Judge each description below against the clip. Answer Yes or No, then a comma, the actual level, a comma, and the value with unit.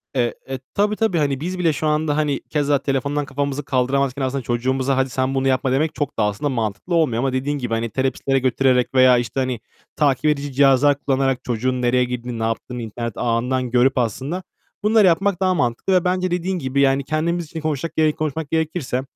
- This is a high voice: No, low, 135 Hz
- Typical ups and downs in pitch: Yes, average, 3.4 semitones